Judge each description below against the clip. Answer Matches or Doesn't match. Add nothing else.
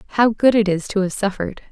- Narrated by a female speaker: Matches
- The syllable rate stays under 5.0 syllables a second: Doesn't match